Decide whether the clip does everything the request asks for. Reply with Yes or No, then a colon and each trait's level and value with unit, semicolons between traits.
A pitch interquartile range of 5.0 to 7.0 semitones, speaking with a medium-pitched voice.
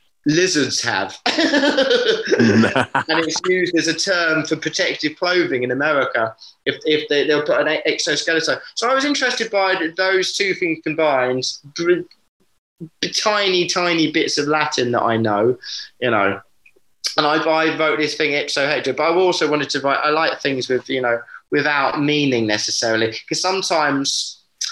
Yes: average, 5.3 semitones; medium, 160 Hz